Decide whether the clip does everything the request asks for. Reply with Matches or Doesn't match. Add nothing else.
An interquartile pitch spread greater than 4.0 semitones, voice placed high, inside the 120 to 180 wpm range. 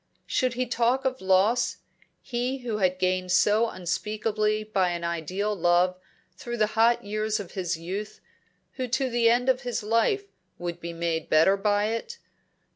Matches